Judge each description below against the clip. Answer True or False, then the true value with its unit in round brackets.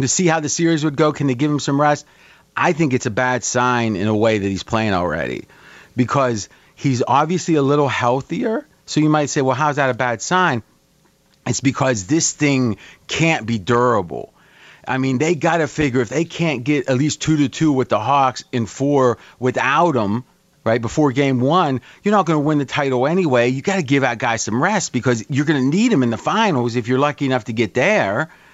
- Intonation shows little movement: False (3.6 semitones)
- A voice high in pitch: False (135 Hz)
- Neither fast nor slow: False (225 wpm)